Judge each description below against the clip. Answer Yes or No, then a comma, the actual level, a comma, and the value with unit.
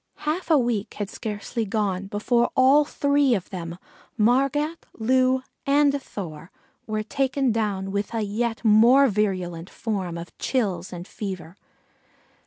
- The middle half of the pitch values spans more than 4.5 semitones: Yes, average, 5.2 semitones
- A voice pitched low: No, high, 215 Hz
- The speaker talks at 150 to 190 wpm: No, slow, 135 wpm